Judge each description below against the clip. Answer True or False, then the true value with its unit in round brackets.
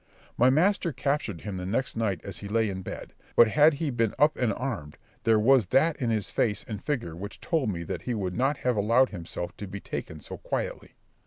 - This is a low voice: True (115 Hz)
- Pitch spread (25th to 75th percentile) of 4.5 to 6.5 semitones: True (5.2 semitones)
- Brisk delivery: True (225 wpm)